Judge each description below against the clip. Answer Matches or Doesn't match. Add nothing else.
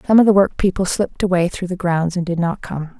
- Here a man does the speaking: Doesn't match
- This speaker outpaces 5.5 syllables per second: Matches